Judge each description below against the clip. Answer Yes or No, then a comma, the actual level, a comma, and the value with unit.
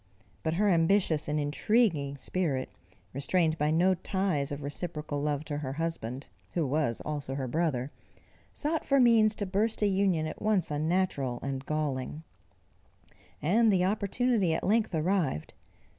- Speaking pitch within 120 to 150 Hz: No, medium, 160 Hz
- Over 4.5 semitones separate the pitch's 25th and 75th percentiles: Yes, average, 5.2 semitones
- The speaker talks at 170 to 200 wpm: No, average, 145 wpm